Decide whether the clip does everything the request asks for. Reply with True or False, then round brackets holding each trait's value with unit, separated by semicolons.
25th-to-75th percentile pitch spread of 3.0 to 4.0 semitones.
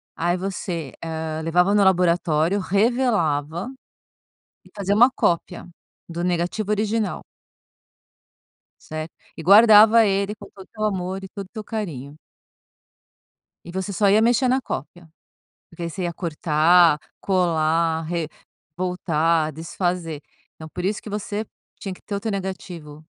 True (3.7 semitones)